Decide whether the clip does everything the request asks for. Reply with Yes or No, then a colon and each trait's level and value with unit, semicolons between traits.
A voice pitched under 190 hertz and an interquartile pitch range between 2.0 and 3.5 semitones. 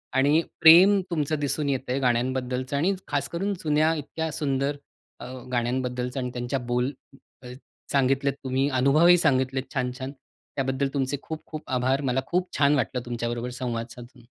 Yes: low, 135 Hz; average, 2.8 semitones